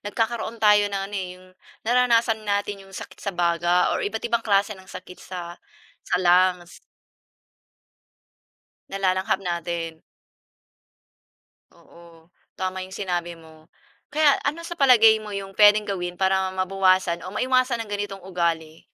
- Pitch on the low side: No, high, 190 Hz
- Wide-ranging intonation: No, average, 3.2 semitones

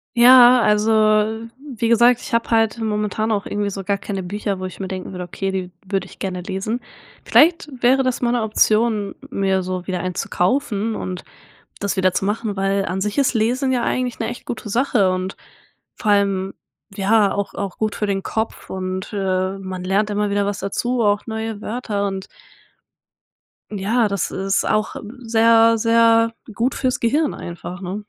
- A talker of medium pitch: No, high, 205 Hz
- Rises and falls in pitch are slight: No, average, 3.0 semitones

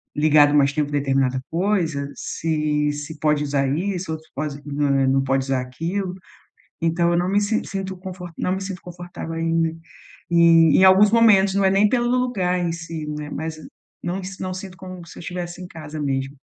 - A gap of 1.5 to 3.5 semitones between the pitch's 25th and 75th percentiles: No, average, 4.0 semitones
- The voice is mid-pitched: Yes, medium, 165 Hz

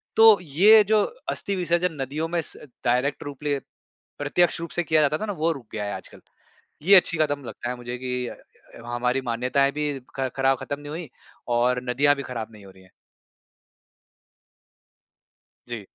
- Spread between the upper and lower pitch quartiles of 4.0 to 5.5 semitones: Yes, average, 4.8 semitones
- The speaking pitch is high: No, medium, 140 Hz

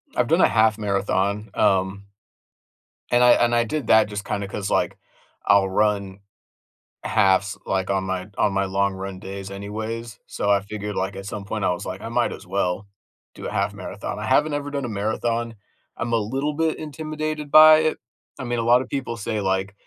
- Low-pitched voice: Yes, low, 105 Hz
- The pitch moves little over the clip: No, average, 3.4 semitones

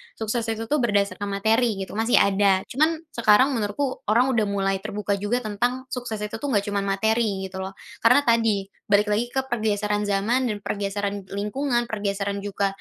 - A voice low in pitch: No, high, 210 Hz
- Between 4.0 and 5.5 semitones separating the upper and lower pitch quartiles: No, average, 3.0 semitones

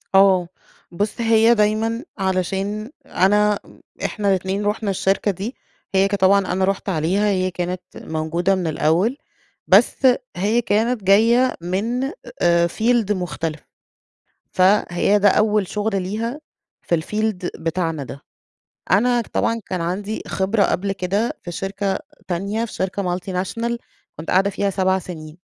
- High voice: Yes, high, 195 Hz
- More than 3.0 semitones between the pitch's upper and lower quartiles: No, average, 2.7 semitones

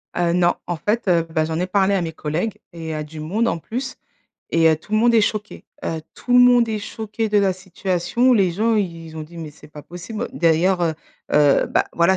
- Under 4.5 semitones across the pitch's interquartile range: No, average, 4.8 semitones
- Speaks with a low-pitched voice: No, medium, 180 Hz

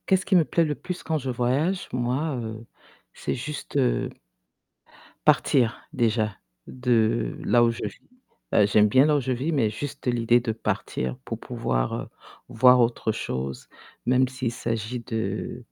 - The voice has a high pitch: No, low, 120 Hz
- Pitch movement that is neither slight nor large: Yes, average, 3.1 semitones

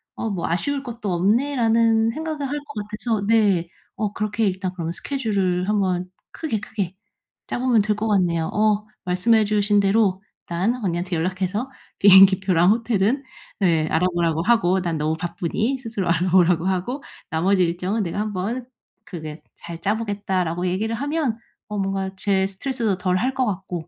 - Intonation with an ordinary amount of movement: Yes, average, 3.9 semitones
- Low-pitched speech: No, high, 200 Hz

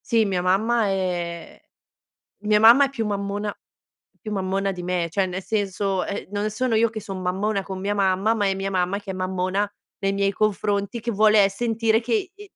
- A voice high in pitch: Yes, high, 200 Hz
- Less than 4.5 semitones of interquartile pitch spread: Yes, narrow, 2.4 semitones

